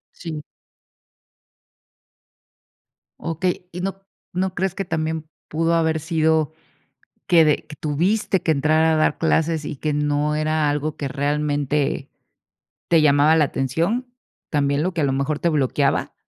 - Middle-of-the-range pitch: Yes, medium, 155 Hz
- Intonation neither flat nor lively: No, narrow, 2.2 semitones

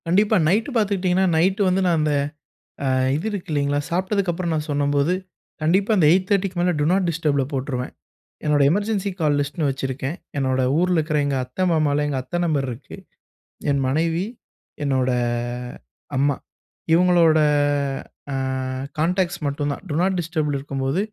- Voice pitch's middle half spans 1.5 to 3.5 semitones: No, average, 4.3 semitones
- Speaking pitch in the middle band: Yes, medium, 160 Hz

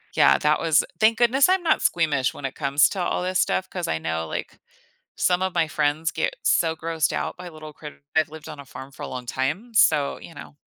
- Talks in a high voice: No, medium, 160 Hz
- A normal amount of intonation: Yes, average, 4.4 semitones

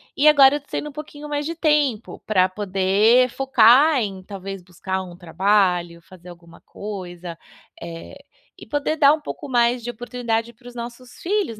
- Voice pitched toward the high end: Yes, high, 230 Hz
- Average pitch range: No, wide, 6.9 semitones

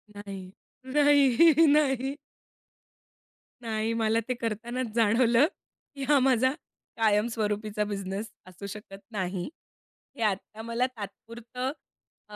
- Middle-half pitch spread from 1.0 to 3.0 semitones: No, average, 3.5 semitones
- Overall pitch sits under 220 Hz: No, high, 225 Hz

